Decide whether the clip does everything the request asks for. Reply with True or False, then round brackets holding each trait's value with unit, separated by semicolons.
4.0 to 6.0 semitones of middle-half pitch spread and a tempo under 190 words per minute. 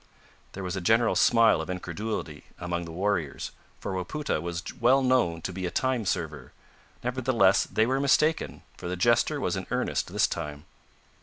True (5.6 semitones; 170 wpm)